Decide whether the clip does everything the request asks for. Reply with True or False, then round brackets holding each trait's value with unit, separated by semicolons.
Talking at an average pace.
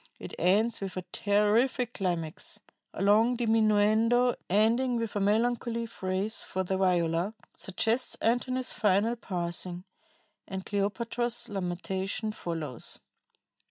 False (110 wpm)